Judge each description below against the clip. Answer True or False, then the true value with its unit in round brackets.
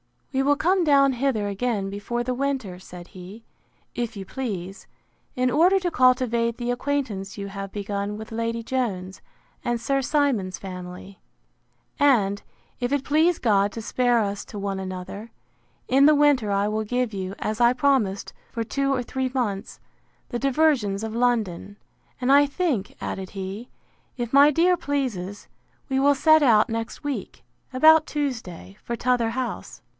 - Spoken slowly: False (160 wpm)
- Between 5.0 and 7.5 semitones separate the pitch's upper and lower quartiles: True (5.3 semitones)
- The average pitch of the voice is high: True (235 Hz)